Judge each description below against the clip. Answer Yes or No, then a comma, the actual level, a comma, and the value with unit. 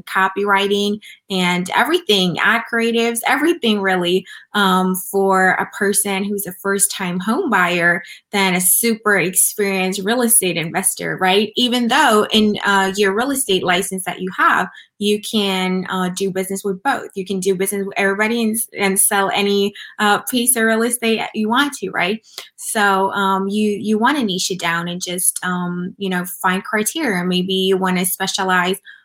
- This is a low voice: No, high, 195 Hz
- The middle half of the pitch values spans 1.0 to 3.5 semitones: Yes, narrow, 2.5 semitones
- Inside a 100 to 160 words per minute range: No, average, 170 wpm